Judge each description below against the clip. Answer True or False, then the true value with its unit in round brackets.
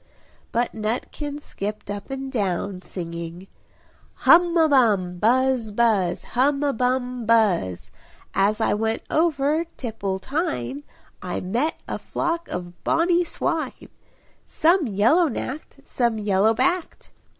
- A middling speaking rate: False (120 wpm)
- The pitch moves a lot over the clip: True (6.6 semitones)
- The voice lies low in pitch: False (235 Hz)